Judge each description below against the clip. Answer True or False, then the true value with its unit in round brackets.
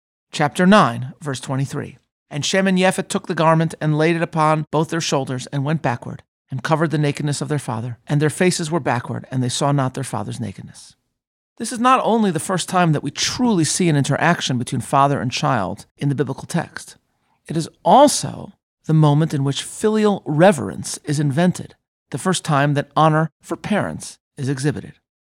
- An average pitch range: True (3.7 semitones)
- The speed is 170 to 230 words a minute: True (195 wpm)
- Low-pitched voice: False (150 Hz)